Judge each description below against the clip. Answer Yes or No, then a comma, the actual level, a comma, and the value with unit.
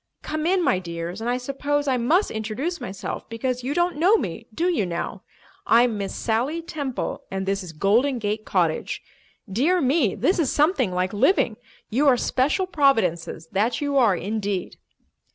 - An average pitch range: No, wide, 6.6 semitones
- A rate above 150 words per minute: Yes, average, 170 wpm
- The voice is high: Yes, high, 245 Hz